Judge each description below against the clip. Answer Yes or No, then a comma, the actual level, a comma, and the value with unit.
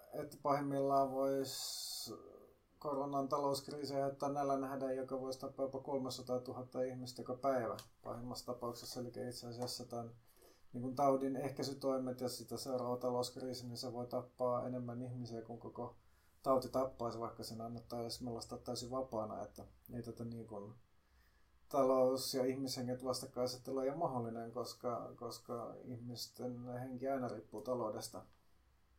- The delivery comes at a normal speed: Yes, average, 135 wpm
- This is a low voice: Yes, low, 125 Hz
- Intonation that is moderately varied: No, narrow, 2.0 semitones